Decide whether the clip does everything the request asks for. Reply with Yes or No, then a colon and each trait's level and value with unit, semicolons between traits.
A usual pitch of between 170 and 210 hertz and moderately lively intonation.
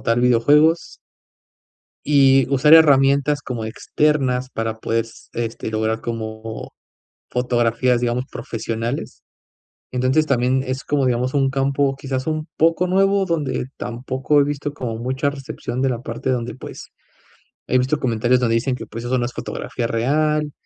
No: low, 130 Hz; average, 3.2 semitones